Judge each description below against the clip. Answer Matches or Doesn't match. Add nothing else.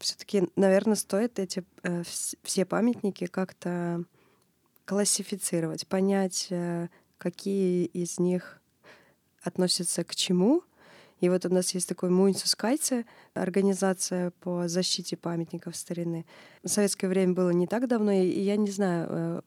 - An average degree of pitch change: Doesn't match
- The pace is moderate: Doesn't match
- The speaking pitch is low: Doesn't match